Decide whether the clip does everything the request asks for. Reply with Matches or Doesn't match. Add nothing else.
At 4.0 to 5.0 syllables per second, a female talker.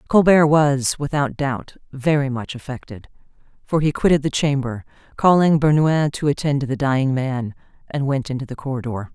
Doesn't match